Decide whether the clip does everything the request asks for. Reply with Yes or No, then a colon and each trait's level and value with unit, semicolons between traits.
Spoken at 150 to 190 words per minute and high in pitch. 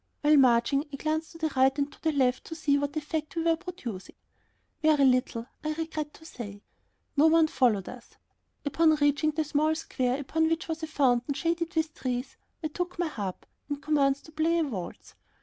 No: average, 200 wpm; very high, 300 Hz